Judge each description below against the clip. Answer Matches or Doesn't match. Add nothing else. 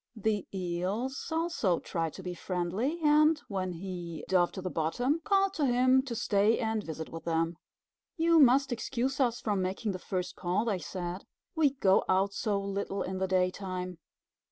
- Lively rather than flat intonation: Matches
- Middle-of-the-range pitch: Doesn't match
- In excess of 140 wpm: Matches